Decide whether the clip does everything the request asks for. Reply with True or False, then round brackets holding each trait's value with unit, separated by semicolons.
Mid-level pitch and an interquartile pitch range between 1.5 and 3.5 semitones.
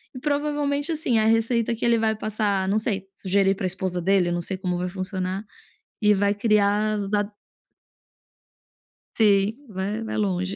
False (205 Hz; 2.8 semitones)